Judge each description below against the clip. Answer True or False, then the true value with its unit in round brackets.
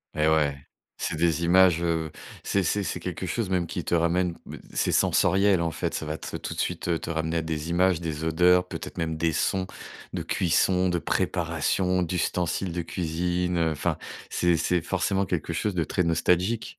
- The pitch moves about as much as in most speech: False (1.9 semitones)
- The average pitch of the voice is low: True (85 Hz)